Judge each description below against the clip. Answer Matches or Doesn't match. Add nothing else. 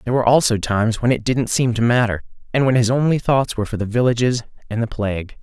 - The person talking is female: Doesn't match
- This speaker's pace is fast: Matches